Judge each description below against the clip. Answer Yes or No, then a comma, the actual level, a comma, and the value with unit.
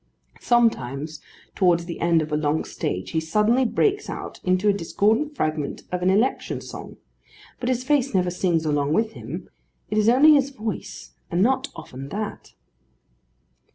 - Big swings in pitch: Yes, wide, 7.1 semitones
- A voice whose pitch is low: No, medium, 185 Hz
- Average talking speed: Yes, average, 160 wpm